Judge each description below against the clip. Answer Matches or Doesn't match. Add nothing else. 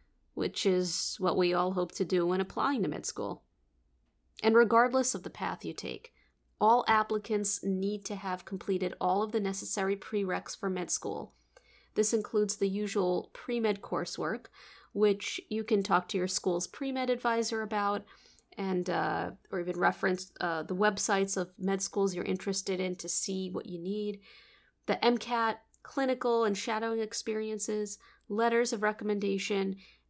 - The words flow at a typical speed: Matches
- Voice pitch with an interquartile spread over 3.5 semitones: Doesn't match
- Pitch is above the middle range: Matches